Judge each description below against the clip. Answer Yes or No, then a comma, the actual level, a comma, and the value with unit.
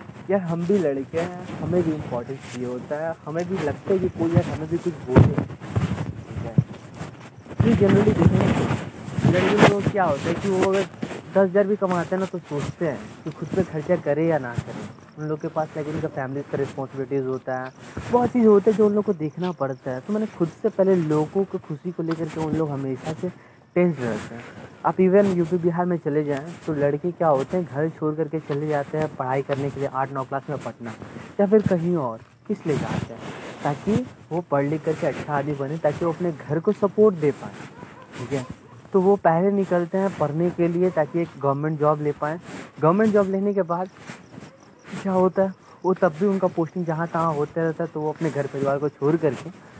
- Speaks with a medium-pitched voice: Yes, medium, 160 Hz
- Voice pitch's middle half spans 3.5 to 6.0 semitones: Yes, average, 4.2 semitones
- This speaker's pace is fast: Yes, fast, 225 wpm